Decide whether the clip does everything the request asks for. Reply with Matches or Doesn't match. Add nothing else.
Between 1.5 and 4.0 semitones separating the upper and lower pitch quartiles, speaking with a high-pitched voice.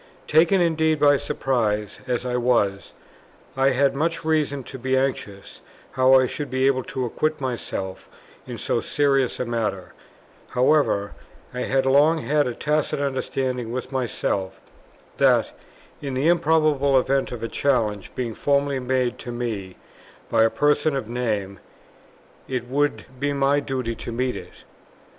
Doesn't match